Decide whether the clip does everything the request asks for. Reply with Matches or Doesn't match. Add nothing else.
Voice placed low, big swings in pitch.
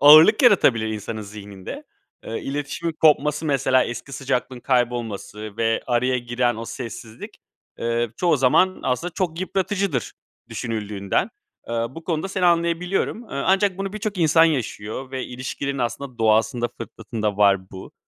Matches